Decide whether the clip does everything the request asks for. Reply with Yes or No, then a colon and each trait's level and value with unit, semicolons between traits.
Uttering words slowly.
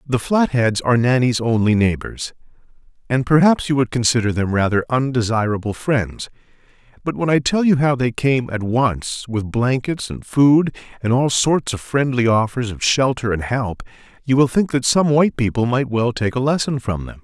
No: average, 185 wpm